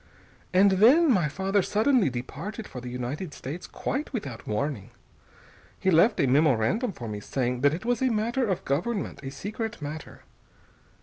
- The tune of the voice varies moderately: No, wide, 8.4 semitones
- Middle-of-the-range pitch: Yes, medium, 175 Hz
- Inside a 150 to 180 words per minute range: Yes, average, 165 wpm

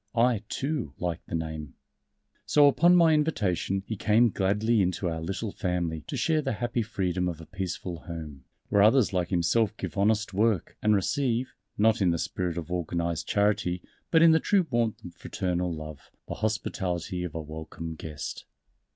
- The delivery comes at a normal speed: Yes, average, 175 wpm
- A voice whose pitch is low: Yes, very low, 95 Hz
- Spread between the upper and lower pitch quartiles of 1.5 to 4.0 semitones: No, average, 4.9 semitones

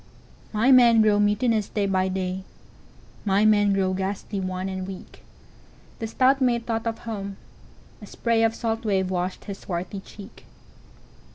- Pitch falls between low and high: No, high, 205 Hz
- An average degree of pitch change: Yes, average, 3.0 semitones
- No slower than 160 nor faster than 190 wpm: No, slow, 135 wpm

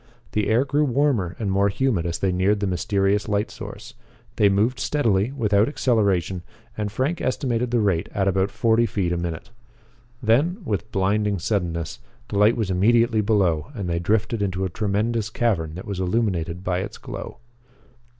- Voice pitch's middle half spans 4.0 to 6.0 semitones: No, average, 3.6 semitones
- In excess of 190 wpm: No, average, 170 wpm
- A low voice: Yes, low, 100 Hz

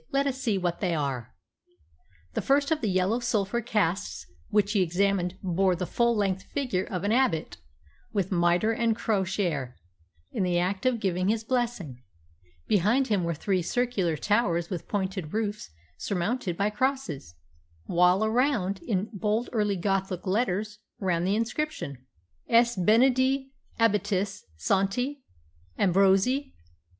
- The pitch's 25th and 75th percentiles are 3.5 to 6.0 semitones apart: Yes, average, 4.4 semitones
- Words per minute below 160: Yes, average, 140 wpm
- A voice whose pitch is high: Yes, high, 200 Hz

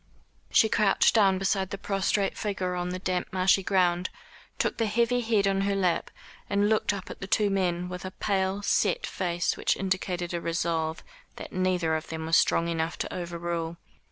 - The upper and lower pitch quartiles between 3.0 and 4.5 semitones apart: No, narrow, 2.4 semitones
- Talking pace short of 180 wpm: No, average, 185 wpm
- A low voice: No, medium, 185 Hz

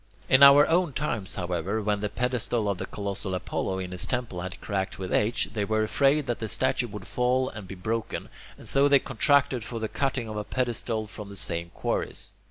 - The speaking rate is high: Yes, fast, 210 wpm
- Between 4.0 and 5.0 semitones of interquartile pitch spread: Yes, average, 4.5 semitones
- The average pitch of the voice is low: Yes, low, 110 Hz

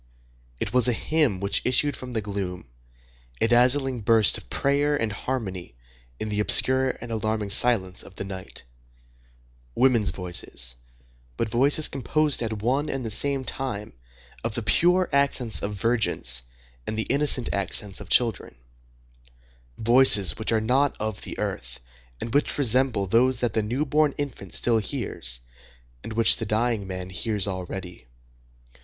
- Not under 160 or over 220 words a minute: No, average, 150 wpm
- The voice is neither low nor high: No, low, 110 Hz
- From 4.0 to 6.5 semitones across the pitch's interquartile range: Yes, average, 5.0 semitones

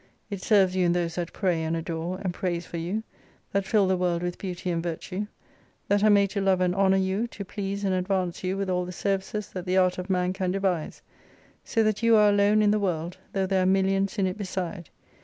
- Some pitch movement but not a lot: No, narrow, 1.9 semitones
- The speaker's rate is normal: No, fast, 235 wpm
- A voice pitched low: No, high, 190 Hz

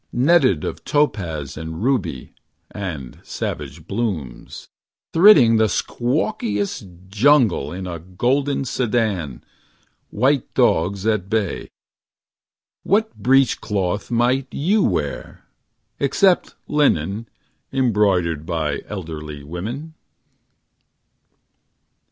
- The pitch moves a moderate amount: No, wide, 7.7 semitones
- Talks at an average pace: No, slow, 85 wpm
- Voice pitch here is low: Yes, low, 105 Hz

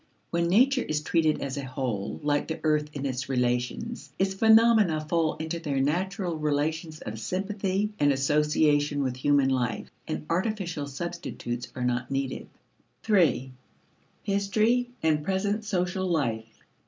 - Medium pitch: Yes, medium, 155 Hz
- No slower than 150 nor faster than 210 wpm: No, average, 140 wpm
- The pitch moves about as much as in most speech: No, wide, 5.8 semitones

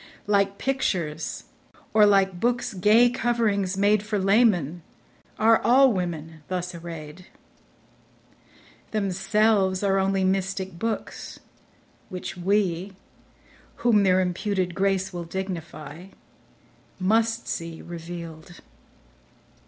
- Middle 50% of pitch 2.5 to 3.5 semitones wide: Yes, average, 3.2 semitones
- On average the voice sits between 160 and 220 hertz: Yes, high, 190 Hz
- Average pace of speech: No, slow, 90 wpm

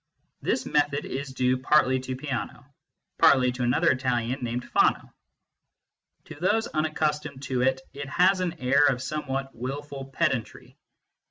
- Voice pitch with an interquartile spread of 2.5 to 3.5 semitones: Yes, average, 2.8 semitones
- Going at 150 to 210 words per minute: No, average, 140 wpm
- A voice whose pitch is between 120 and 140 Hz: Yes, low, 135 Hz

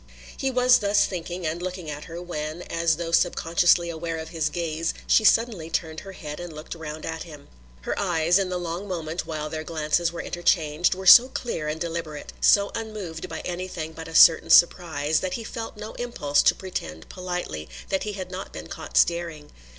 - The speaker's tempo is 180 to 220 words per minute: Yes, average, 200 wpm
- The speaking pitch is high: No, medium, 170 Hz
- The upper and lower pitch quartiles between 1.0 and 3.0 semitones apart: Yes, narrow, 2.6 semitones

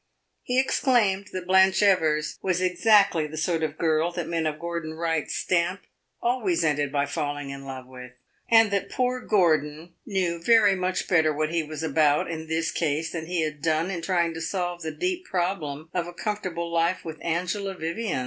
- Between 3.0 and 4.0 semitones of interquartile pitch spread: Yes, average, 3.3 semitones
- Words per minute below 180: No, average, 185 wpm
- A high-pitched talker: No, medium, 170 Hz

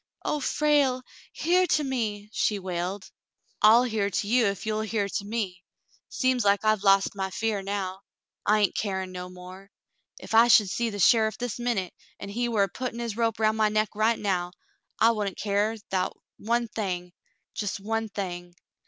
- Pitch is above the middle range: Yes, high, 210 Hz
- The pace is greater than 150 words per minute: Yes, average, 190 wpm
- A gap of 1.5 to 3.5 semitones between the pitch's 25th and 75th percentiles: Yes, average, 2.8 semitones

